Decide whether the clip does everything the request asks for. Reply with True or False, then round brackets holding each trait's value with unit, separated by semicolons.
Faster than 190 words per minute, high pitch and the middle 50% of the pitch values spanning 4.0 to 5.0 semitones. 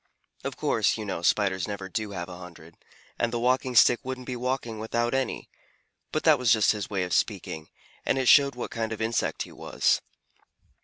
False (200 wpm; 110 Hz; 4.7 semitones)